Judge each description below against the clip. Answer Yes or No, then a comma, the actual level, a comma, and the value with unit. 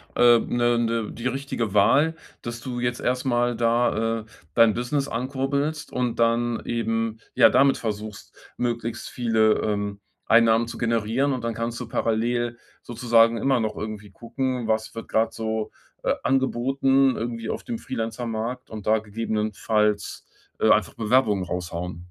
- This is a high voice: No, low, 115 Hz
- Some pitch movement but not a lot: No, narrow, 1.9 semitones